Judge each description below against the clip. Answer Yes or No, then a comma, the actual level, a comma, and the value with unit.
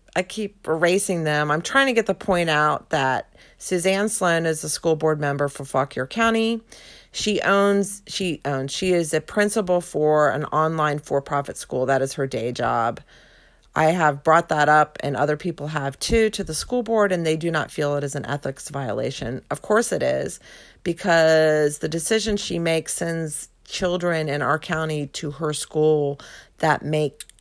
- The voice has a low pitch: No, medium, 160 Hz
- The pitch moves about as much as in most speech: Yes, average, 3.7 semitones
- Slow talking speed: No, average, 185 wpm